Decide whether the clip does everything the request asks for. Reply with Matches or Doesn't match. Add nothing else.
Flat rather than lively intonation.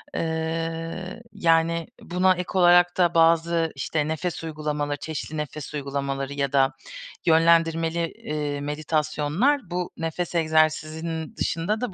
Matches